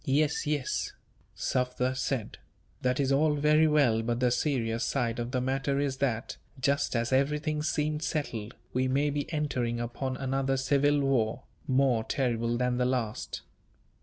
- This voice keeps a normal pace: Yes, average, 155 wpm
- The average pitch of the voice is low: Yes, low, 130 Hz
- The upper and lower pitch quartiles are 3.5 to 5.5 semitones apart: No, average, 2.8 semitones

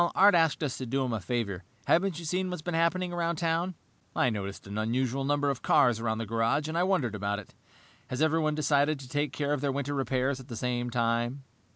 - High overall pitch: No, low, 135 Hz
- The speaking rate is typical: No, fast, 230 wpm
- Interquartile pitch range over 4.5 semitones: Yes, average, 5.2 semitones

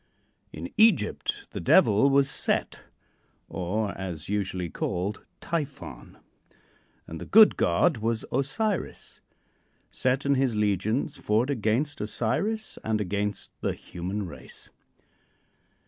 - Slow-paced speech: Yes, slow, 110 wpm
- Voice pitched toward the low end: Yes, low, 110 Hz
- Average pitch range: No, wide, 5.7 semitones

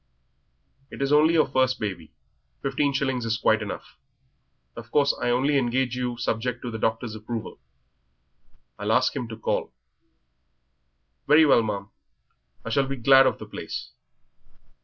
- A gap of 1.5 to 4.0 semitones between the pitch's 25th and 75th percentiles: Yes, average, 3.4 semitones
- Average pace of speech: Yes, average, 150 wpm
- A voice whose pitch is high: No, low, 125 Hz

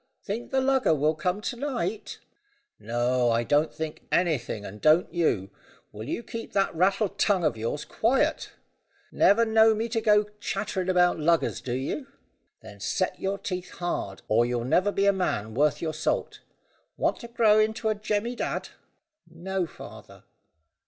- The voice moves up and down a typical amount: No, wide, 6.7 semitones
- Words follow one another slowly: No, average, 165 wpm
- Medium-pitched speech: Yes, medium, 180 Hz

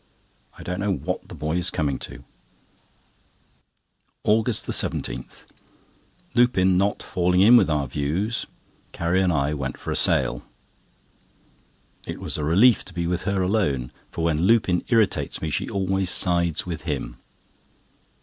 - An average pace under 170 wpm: Yes, average, 140 wpm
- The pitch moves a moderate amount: Yes, average, 4.2 semitones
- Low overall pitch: Yes, very low, 90 Hz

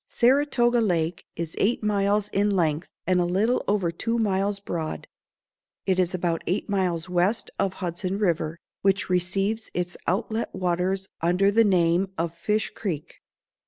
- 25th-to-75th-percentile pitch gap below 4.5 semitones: Yes, average, 3.0 semitones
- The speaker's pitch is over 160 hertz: Yes, high, 190 Hz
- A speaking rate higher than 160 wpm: No, average, 150 wpm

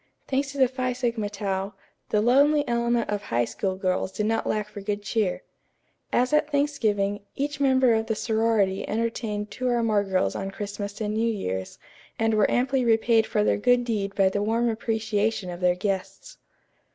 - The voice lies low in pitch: No, high, 220 Hz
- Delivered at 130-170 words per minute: No, average, 185 wpm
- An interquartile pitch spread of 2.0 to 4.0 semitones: Yes, average, 3.0 semitones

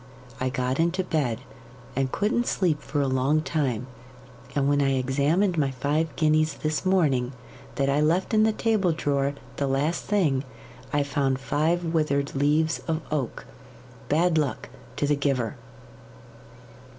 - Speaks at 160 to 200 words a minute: No, average, 150 wpm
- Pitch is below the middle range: No, medium, 145 Hz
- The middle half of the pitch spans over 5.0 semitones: No, average, 3.1 semitones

